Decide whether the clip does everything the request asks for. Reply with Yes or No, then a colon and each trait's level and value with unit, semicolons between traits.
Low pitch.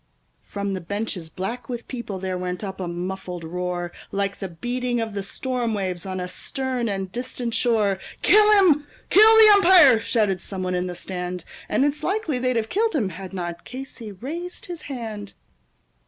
No: high, 215 Hz